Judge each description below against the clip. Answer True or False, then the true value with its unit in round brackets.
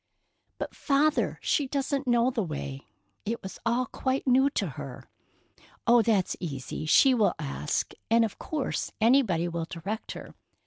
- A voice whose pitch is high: True (230 Hz)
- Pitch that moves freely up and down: True (7.3 semitones)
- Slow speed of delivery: False (150 wpm)